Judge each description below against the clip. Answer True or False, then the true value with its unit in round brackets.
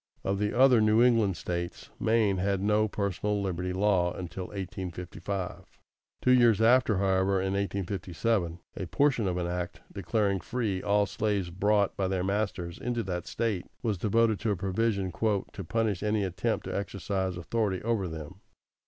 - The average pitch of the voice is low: True (100 Hz)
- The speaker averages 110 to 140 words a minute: False (160 wpm)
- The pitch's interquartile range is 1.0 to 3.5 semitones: True (2.8 semitones)